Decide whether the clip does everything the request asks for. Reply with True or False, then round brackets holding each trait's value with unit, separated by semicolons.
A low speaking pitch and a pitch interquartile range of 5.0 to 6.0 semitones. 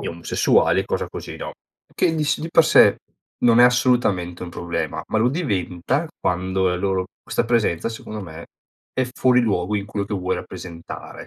True (100 Hz; 5.6 semitones)